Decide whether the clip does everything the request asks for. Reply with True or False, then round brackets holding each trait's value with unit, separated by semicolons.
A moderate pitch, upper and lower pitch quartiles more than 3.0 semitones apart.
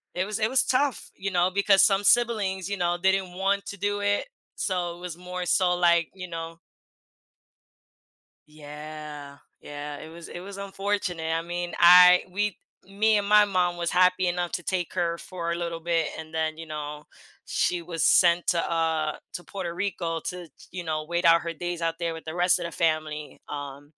False (175 Hz; 2.5 semitones)